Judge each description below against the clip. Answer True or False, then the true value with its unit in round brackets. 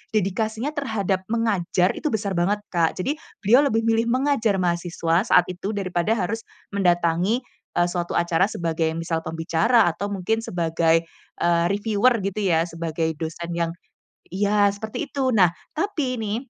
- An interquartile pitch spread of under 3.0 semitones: False (4.6 semitones)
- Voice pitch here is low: False (195 Hz)